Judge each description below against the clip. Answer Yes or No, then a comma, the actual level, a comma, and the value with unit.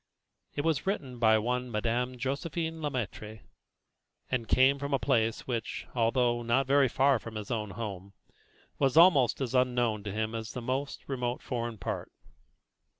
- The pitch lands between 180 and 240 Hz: No, low, 125 Hz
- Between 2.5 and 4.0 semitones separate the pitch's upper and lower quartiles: Yes, average, 3.2 semitones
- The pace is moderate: Yes, average, 160 wpm